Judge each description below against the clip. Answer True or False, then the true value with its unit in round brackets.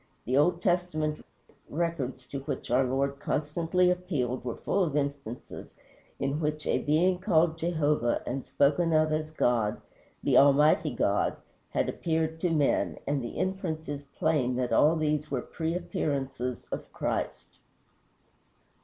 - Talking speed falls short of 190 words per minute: True (145 wpm)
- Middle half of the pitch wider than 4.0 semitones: False (3.3 semitones)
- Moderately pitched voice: True (150 Hz)